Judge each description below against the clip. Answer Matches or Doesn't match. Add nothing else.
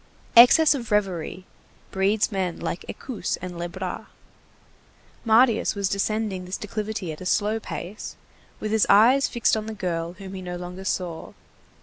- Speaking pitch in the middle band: Doesn't match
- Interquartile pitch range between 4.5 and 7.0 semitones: Doesn't match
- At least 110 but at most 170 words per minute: Matches